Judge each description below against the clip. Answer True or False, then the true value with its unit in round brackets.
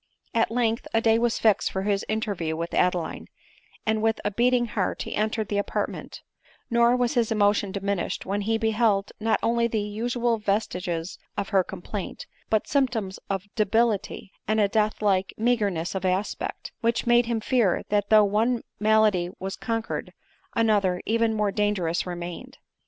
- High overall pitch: True (215 Hz)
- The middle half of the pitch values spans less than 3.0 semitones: True (2.6 semitones)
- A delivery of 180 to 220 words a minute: False (165 wpm)